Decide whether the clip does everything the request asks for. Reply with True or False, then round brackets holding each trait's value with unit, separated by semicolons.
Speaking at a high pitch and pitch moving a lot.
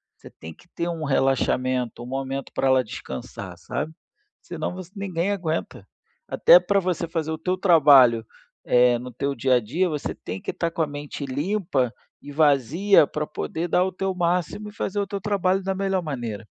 False (155 Hz; 5.9 semitones)